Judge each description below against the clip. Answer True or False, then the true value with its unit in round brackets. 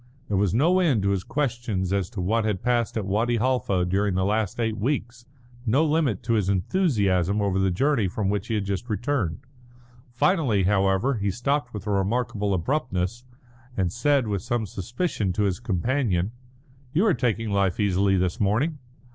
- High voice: False (105 Hz)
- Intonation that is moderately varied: True (4.2 semitones)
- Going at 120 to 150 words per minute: False (180 wpm)